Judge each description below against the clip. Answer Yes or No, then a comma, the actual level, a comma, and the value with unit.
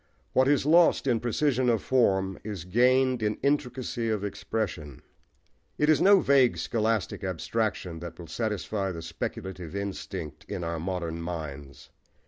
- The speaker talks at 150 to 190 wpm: No, average, 140 wpm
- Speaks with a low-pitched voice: Yes, low, 105 Hz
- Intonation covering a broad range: Yes, wide, 6.5 semitones